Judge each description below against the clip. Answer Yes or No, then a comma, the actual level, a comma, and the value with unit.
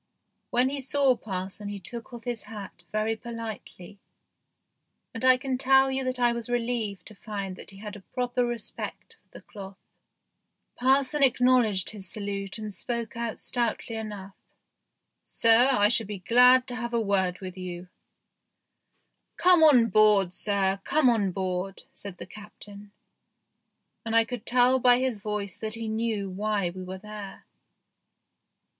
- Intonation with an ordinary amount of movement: Yes, average, 3.6 semitones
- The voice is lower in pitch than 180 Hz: No, high, 220 Hz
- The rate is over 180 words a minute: No, average, 160 wpm